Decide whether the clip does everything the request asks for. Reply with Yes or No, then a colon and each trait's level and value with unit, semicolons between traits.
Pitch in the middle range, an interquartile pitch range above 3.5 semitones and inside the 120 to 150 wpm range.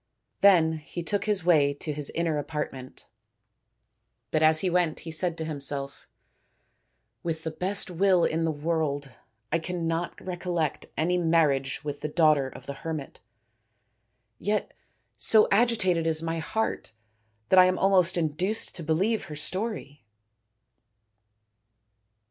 No: medium, 165 Hz; average, 3.2 semitones; slow, 135 wpm